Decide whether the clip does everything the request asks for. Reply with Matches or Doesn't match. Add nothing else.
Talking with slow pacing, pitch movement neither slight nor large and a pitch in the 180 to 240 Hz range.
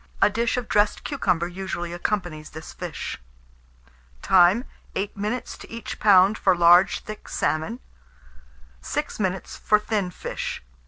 Matches